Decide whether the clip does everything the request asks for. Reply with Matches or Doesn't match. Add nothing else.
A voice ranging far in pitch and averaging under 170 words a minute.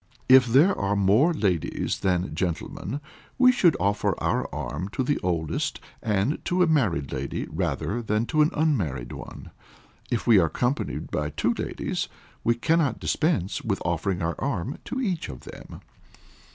Matches